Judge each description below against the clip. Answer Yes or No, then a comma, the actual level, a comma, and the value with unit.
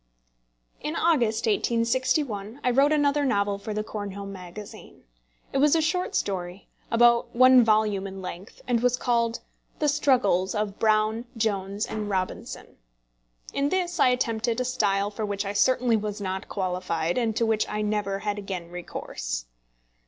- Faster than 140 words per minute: Yes, average, 155 wpm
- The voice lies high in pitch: Yes, high, 215 Hz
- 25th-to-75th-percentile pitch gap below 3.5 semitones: No, average, 3.9 semitones